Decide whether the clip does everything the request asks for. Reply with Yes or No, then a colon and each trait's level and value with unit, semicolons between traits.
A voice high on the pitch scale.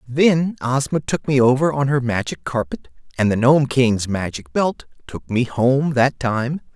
No: low, 125 Hz